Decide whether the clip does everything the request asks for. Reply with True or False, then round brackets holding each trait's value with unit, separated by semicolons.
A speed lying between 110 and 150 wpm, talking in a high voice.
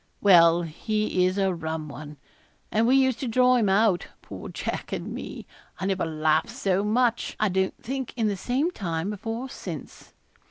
False (185 wpm; 200 Hz)